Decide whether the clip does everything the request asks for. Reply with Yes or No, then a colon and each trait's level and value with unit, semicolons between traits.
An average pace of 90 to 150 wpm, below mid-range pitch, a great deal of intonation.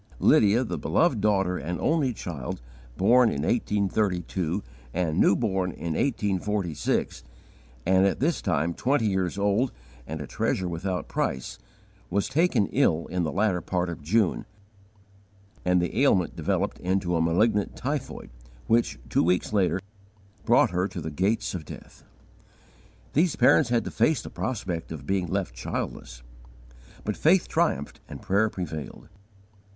No: average, 145 wpm; very low, 95 Hz; average, 4.6 semitones